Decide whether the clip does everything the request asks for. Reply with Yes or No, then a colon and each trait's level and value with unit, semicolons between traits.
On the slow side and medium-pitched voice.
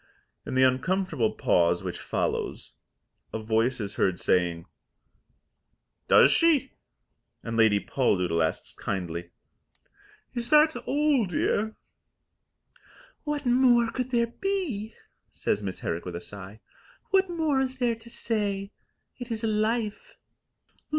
No: slow, 120 wpm; high, 210 Hz